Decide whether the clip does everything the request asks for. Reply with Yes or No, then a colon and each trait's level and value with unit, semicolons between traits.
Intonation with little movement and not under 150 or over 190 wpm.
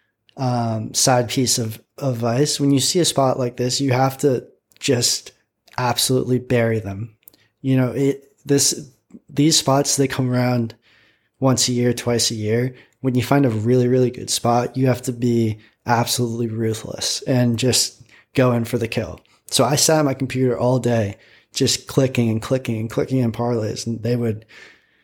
Yes: narrow, 2.2 semitones; average, 180 wpm